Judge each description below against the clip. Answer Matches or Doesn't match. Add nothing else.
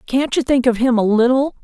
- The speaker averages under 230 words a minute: Doesn't match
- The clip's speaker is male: Doesn't match